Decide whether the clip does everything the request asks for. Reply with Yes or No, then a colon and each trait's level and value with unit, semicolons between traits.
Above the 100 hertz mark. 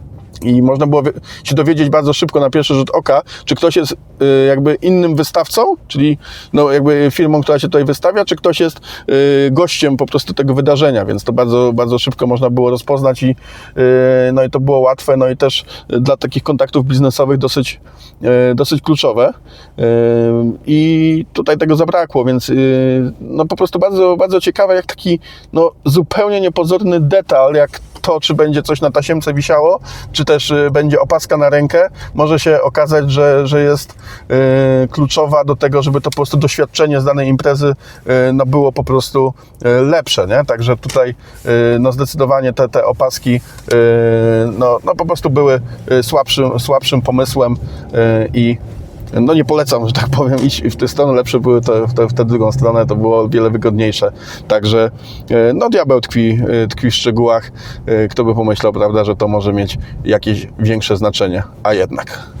Yes: low, 135 Hz